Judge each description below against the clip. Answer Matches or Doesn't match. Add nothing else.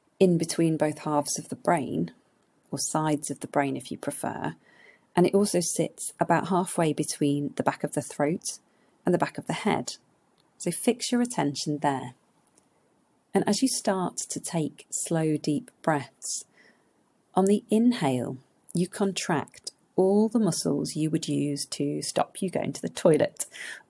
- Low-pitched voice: Doesn't match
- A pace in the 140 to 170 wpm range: Matches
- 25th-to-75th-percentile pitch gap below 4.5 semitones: Doesn't match